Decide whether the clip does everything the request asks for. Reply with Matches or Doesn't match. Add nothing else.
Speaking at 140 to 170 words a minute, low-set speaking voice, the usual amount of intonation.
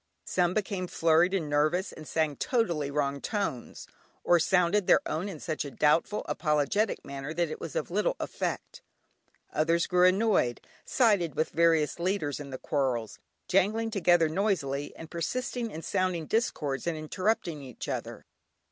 Doesn't match